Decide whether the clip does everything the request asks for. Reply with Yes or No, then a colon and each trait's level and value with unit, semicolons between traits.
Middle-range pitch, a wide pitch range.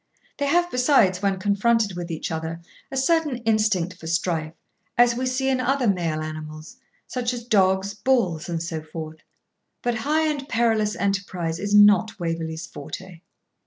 No: high, 200 Hz; wide, 6.5 semitones